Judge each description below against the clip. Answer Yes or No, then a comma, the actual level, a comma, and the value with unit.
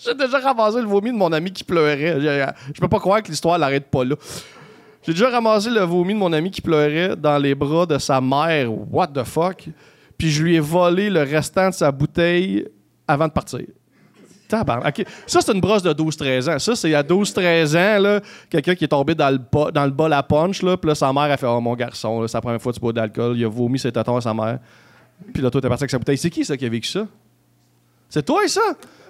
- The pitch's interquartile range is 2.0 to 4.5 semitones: No, average, 5.3 semitones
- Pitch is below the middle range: No, medium, 155 Hz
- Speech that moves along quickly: Yes, fast, 245 wpm